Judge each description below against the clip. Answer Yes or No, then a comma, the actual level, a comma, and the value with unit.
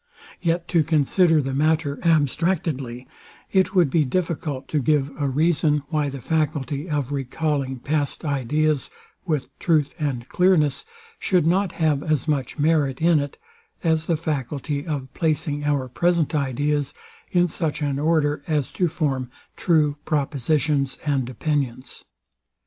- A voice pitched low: No, medium, 150 Hz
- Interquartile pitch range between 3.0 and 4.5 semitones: No, narrow, 2.6 semitones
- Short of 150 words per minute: Yes, average, 140 wpm